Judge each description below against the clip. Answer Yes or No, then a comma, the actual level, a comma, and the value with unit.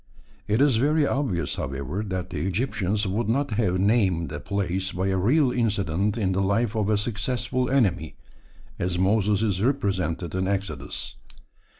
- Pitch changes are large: No, average, 3.6 semitones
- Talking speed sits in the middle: Yes, average, 160 wpm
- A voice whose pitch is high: No, low, 100 Hz